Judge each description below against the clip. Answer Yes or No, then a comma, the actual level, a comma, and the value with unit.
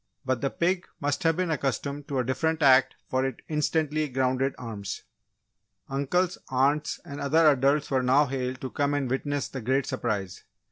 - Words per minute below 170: No, average, 175 wpm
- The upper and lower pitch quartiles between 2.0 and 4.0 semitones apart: Yes, narrow, 2.4 semitones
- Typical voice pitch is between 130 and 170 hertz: Yes, medium, 140 Hz